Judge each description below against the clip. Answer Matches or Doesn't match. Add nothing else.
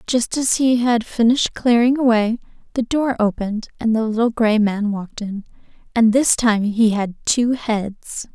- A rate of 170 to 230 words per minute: Matches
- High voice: Matches